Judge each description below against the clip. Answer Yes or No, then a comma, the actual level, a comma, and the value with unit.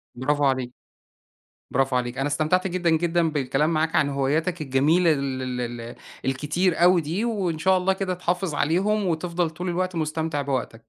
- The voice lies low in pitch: No, medium, 160 Hz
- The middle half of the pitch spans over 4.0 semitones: Yes, average, 4.6 semitones